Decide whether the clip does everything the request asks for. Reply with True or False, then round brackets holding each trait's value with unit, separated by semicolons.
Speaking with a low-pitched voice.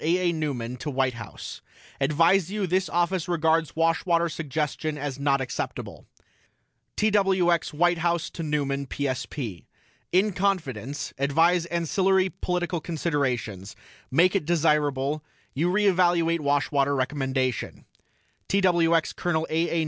False (160 Hz)